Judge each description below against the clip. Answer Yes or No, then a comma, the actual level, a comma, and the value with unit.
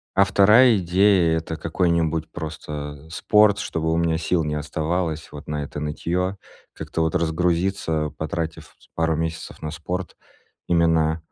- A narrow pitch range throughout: Yes, narrow, 2.2 semitones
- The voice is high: No, very low, 80 Hz